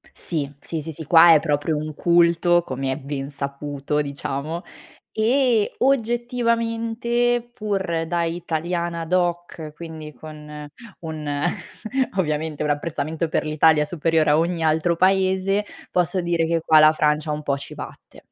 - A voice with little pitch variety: No, average, 3.1 semitones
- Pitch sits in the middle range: Yes, medium, 165 Hz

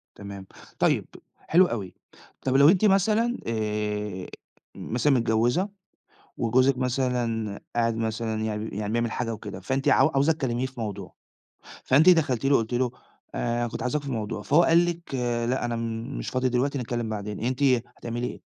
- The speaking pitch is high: No, low, 120 Hz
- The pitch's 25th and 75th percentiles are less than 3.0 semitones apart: No, average, 3.8 semitones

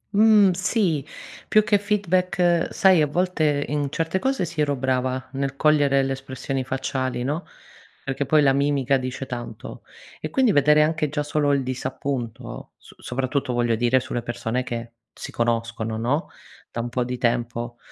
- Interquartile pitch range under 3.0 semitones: No, average, 4.0 semitones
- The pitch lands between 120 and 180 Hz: Yes, low, 135 Hz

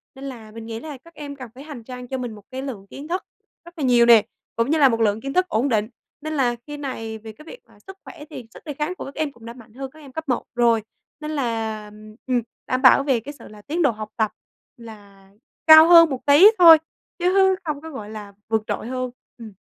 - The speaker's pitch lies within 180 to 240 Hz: No, very high, 255 Hz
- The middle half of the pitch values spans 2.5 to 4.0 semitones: No, average, 5.1 semitones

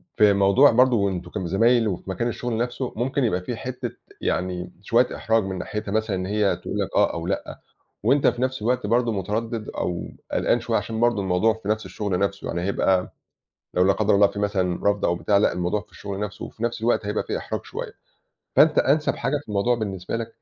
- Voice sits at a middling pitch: No, low, 105 Hz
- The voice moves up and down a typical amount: Yes, average, 3.3 semitones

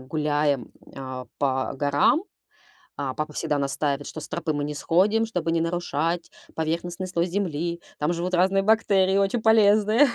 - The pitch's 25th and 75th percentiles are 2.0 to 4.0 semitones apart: No, average, 4.8 semitones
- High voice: No, medium, 170 Hz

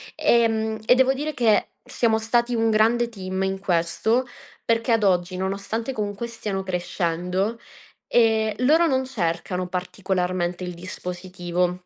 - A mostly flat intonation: No, average, 4.3 semitones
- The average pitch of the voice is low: No, high, 205 Hz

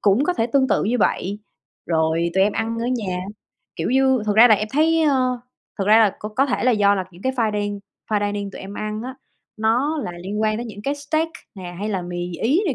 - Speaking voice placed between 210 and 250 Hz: Yes, high, 220 Hz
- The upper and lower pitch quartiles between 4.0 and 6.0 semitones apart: Yes, average, 4.4 semitones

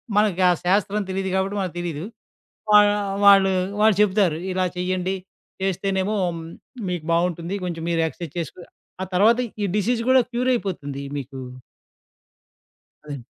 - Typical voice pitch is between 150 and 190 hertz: Yes, medium, 185 Hz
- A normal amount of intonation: Yes, average, 3.2 semitones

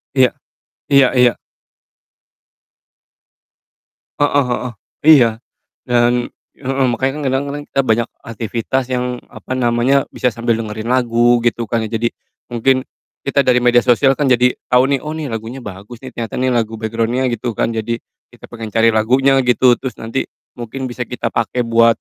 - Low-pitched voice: Yes, low, 120 Hz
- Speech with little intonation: Yes, narrow, 2.2 semitones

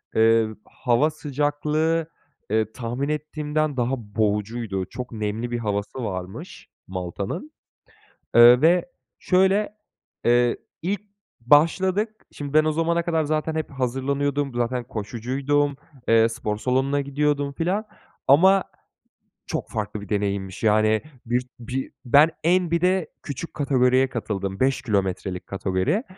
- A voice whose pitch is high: No, low, 130 Hz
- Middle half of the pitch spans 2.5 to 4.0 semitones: No, wide, 5.6 semitones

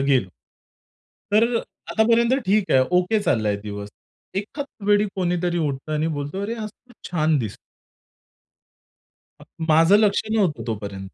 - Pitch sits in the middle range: Yes, medium, 175 Hz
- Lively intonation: Yes, wide, 7.8 semitones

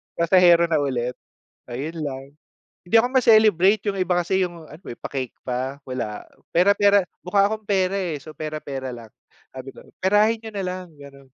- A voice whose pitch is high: No, medium, 170 Hz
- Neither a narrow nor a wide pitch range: No, wide, 6.3 semitones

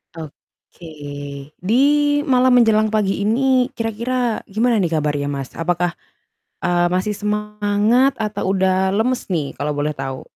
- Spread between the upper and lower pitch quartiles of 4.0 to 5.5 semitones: Yes, average, 4.5 semitones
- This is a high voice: Yes, high, 205 Hz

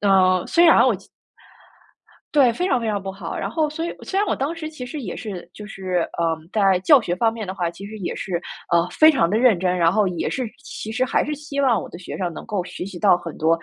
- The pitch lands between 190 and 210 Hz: Yes, high, 205 Hz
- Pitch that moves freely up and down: Yes, wide, 6.7 semitones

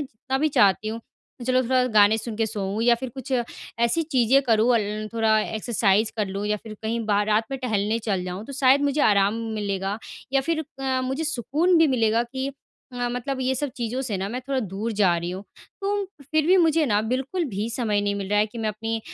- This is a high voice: Yes, high, 230 Hz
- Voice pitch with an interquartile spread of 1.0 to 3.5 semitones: No, average, 4.1 semitones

